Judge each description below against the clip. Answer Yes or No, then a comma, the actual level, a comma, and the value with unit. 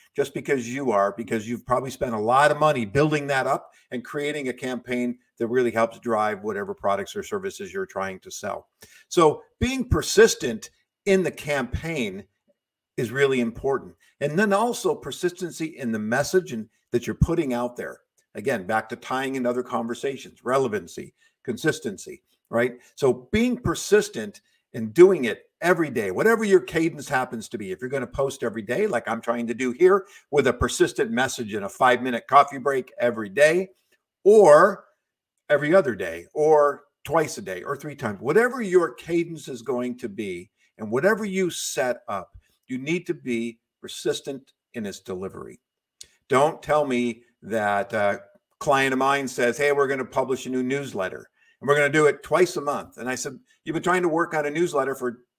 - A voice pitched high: No, medium, 140 Hz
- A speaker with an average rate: Yes, average, 185 wpm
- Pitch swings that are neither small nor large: No, wide, 7.0 semitones